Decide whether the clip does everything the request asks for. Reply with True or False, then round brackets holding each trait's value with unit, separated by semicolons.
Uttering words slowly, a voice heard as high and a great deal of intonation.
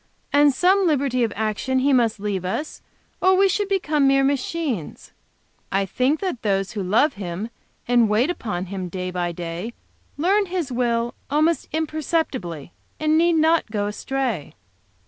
False (155 wpm; 255 Hz; 7.7 semitones)